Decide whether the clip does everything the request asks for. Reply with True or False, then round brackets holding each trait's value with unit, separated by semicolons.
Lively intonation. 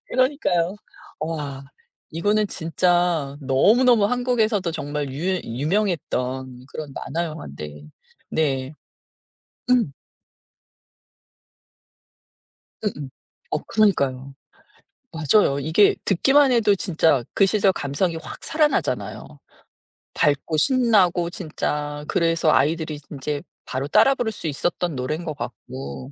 True (6.4 semitones)